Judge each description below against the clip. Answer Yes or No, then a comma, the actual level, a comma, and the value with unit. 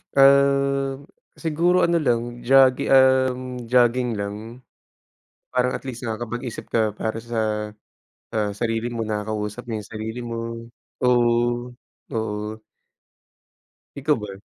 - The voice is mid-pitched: No, low, 120 Hz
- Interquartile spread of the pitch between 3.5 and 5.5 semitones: No, average, 3.0 semitones